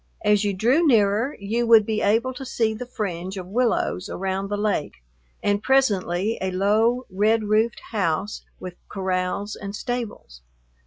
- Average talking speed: Yes, average, 155 wpm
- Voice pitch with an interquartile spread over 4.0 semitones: No, average, 3.2 semitones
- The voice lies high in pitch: Yes, high, 210 Hz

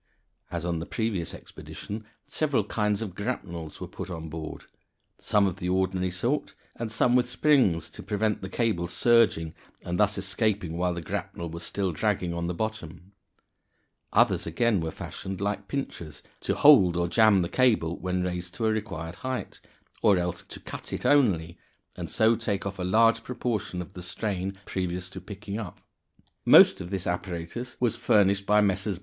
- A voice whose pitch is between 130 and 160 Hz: No, very low, 95 Hz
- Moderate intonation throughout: Yes, average, 3.9 semitones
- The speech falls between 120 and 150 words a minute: No, average, 175 wpm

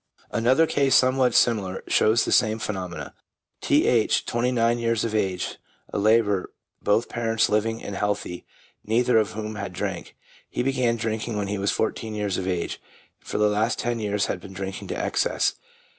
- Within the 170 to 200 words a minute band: Yes, average, 175 wpm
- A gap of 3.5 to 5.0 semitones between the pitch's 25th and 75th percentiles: No, narrow, 2.5 semitones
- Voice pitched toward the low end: Yes, low, 110 Hz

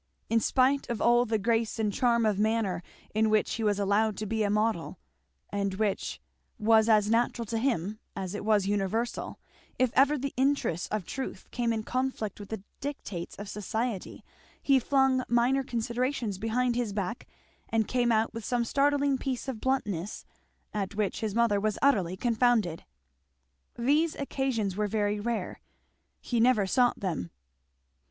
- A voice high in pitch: Yes, high, 225 Hz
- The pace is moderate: Yes, average, 160 wpm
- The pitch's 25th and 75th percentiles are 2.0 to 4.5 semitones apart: Yes, average, 3.3 semitones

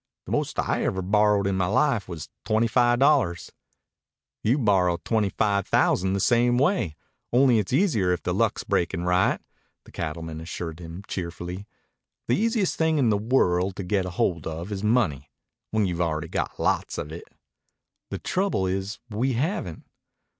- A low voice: Yes, low, 100 Hz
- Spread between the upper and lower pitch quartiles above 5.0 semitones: Yes, wide, 5.5 semitones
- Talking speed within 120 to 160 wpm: No, average, 170 wpm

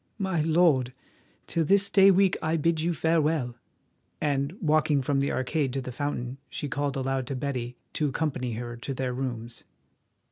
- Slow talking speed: No, average, 170 wpm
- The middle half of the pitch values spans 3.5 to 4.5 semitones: Yes, average, 3.9 semitones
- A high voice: No, medium, 140 Hz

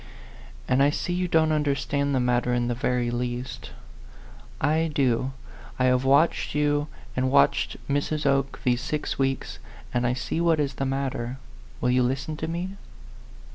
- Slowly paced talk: No, average, 165 wpm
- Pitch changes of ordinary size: Yes, average, 3.0 semitones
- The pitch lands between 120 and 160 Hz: Yes, low, 135 Hz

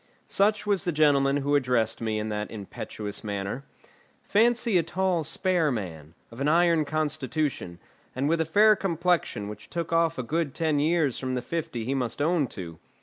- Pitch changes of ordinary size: No, wide, 6.6 semitones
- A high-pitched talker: No, medium, 145 Hz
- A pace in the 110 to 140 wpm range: No, average, 180 wpm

